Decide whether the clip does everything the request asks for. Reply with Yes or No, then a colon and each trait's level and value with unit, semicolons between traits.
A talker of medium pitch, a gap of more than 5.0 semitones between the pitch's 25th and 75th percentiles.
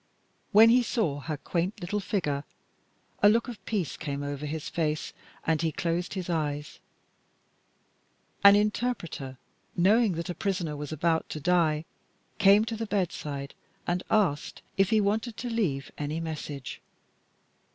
Yes: medium, 170 Hz; wide, 5.5 semitones